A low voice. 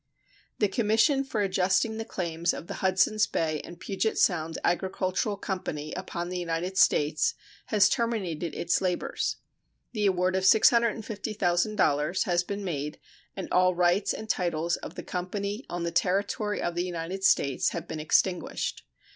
No: medium, 185 Hz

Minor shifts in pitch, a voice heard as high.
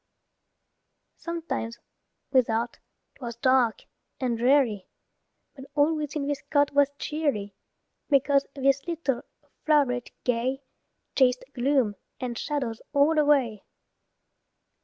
No: average, 3.2 semitones; very high, 270 Hz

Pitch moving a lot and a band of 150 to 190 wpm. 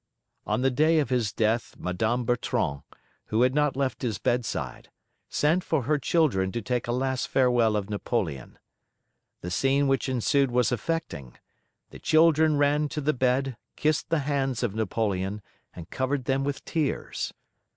No: average, 4.4 semitones; average, 160 wpm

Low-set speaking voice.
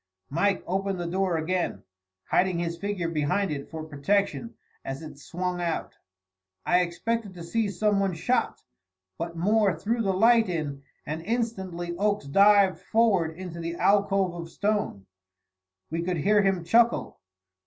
No: medium, 185 Hz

